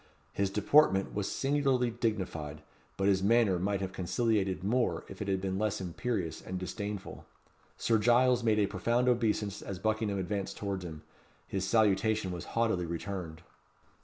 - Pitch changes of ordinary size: Yes, average, 3.3 semitones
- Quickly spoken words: No, average, 155 wpm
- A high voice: No, low, 100 Hz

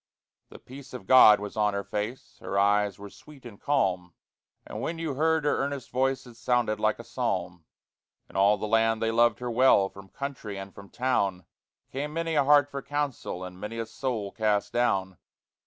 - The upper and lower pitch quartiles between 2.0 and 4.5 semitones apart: No, average, 5.0 semitones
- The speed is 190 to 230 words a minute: Yes, average, 195 wpm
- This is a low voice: Yes, low, 115 Hz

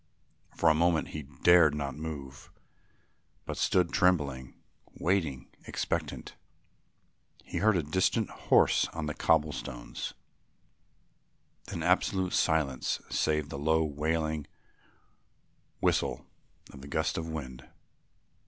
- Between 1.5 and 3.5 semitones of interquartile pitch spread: Yes, average, 2.7 semitones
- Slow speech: Yes, slow, 110 wpm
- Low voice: Yes, very low, 80 Hz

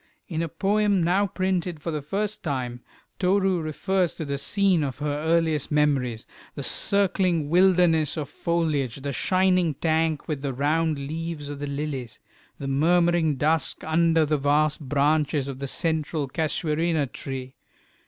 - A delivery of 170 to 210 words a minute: No, average, 150 wpm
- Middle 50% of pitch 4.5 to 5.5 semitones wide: No, average, 3.3 semitones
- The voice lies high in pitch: No, medium, 155 Hz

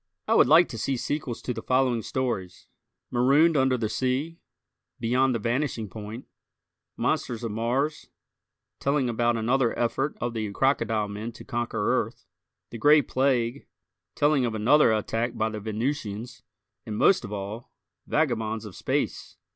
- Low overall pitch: Yes, low, 120 Hz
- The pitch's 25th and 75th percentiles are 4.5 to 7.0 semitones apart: No, average, 3.2 semitones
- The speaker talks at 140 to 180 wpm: Yes, average, 150 wpm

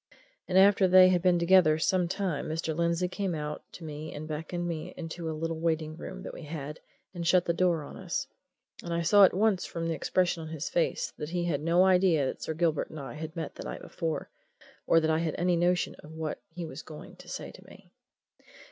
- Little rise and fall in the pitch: Yes, narrow, 2.3 semitones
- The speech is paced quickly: Yes, fast, 230 wpm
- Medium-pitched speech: Yes, medium, 165 Hz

